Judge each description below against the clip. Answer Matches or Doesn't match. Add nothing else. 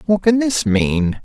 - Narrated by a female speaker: Doesn't match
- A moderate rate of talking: Matches